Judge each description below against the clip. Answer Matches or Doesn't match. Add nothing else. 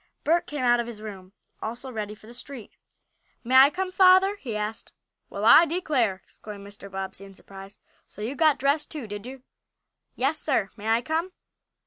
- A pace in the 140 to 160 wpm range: Doesn't match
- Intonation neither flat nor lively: Doesn't match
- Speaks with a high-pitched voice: Matches